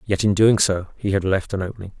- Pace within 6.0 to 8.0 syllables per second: Yes, 6.3 syllables/s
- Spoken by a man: Yes, male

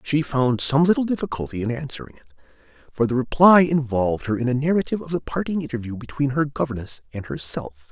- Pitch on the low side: Yes, low, 130 Hz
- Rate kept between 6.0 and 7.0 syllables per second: Yes, 6.4 syllables/s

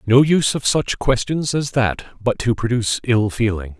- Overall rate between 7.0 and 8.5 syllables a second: No, 4.9 syllables/s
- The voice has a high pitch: No, low, 120 Hz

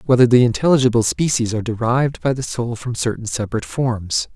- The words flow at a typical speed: Yes, average, 180 wpm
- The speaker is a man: Yes, male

